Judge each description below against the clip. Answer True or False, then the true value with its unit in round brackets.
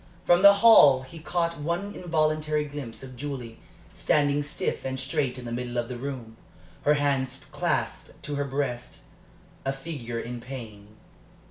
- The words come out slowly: False (160 wpm)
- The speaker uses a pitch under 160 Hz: True (140 Hz)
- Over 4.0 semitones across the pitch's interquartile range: False (3.6 semitones)